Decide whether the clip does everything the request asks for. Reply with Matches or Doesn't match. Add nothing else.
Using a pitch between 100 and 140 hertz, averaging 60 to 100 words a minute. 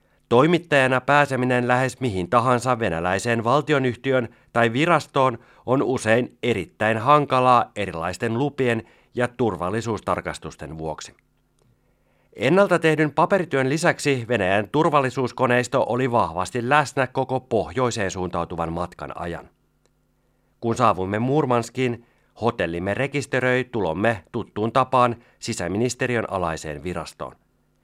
Matches